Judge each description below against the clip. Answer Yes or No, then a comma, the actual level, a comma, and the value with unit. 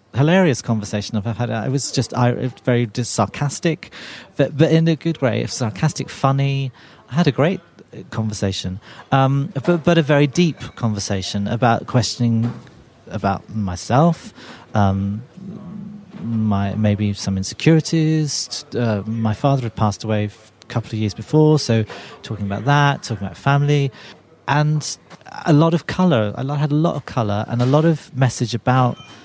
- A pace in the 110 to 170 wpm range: Yes, average, 155 wpm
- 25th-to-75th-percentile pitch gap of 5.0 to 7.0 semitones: Yes, wide, 5.6 semitones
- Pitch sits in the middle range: No, low, 125 Hz